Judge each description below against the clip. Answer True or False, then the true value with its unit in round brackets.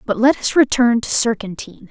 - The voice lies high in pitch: True (230 Hz)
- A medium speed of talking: True (190 wpm)